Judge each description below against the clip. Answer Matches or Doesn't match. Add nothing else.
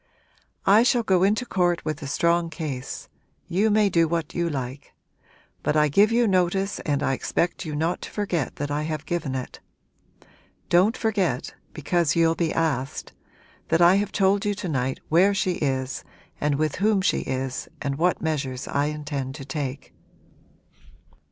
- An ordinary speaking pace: Matches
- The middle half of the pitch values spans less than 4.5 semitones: Doesn't match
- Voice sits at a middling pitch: Matches